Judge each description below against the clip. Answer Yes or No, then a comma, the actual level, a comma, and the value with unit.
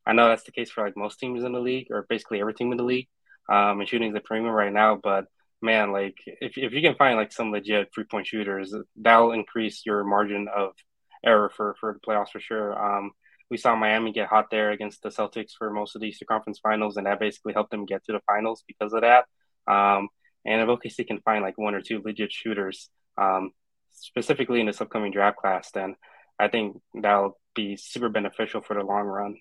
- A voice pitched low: Yes, low, 105 Hz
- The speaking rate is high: Yes, fast, 230 wpm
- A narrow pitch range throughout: Yes, narrow, 1.6 semitones